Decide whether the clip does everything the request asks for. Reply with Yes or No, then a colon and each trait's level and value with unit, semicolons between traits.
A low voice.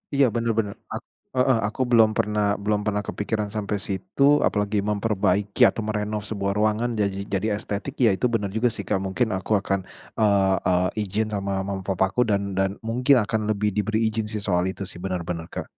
Yes: low, 105 Hz